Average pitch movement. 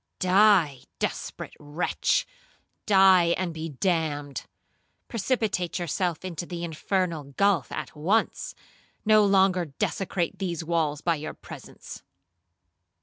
Yes: average, 3.4 semitones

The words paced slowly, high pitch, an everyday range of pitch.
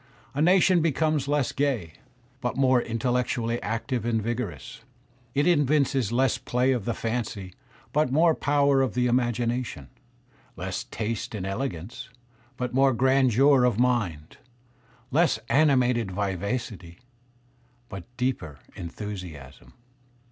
No: slow, 115 wpm; low, 125 Hz; average, 4.2 semitones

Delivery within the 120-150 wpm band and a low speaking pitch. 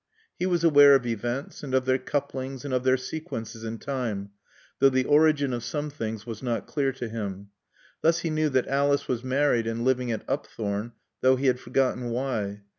No: average, 195 wpm; low, 130 Hz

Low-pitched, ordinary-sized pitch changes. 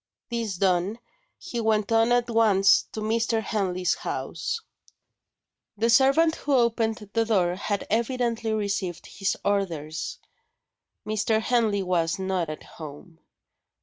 No: high, 215 Hz; average, 3.5 semitones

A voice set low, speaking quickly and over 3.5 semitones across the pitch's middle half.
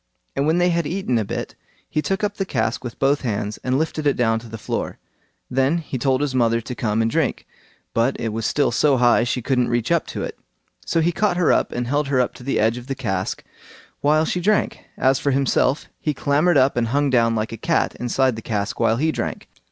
Yes: low, 130 Hz; fast, 240 wpm; average, 4.5 semitones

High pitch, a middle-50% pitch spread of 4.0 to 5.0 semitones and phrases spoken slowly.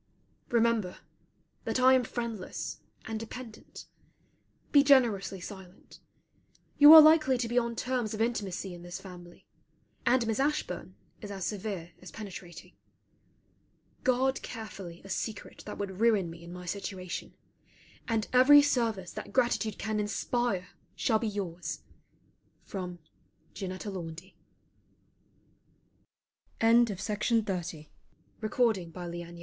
Yes: high, 210 Hz; average, 4.6 semitones; slow, 125 wpm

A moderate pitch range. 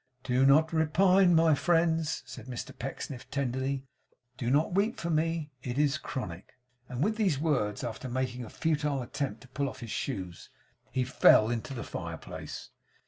Yes: average, 4.4 semitones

